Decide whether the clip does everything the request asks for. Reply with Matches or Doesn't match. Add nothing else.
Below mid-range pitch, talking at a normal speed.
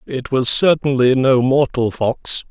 Matches